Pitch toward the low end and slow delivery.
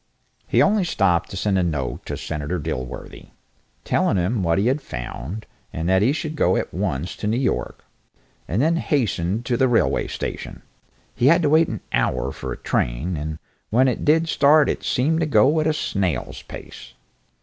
No: low, 110 Hz; average, 190 wpm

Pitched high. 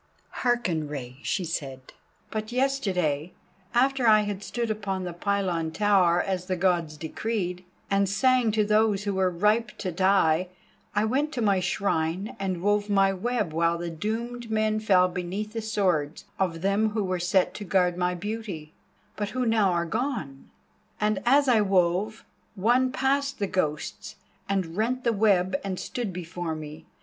Yes: high, 195 Hz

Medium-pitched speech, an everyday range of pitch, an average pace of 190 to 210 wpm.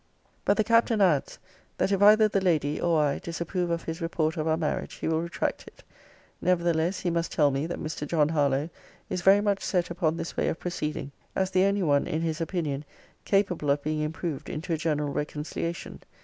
Yes: medium, 165 Hz; average, 3.1 semitones; fast, 205 wpm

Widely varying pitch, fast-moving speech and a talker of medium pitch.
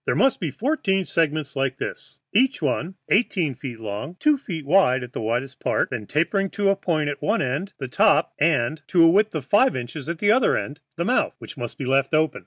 Yes: wide, 6.6 semitones; fast, 230 wpm; medium, 160 Hz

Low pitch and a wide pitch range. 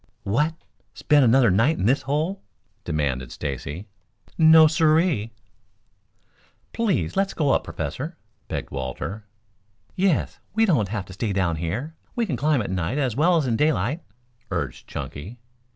Yes: low, 130 Hz; wide, 8.8 semitones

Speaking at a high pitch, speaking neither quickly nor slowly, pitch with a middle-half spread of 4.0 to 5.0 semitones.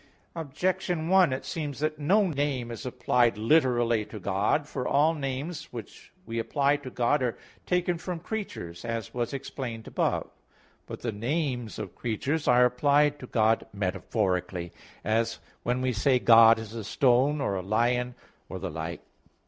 No: low, 125 Hz; average, 165 wpm; average, 4.6 semitones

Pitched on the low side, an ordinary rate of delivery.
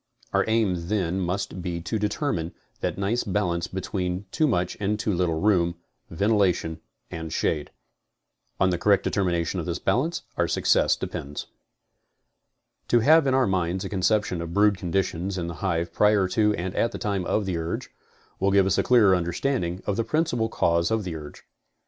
Yes: very low, 95 Hz; average, 180 wpm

